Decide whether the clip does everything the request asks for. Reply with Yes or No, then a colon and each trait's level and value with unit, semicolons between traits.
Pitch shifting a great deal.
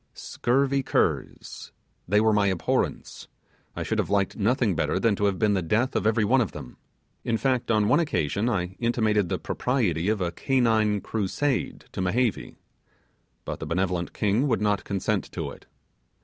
No: average, 3.9 semitones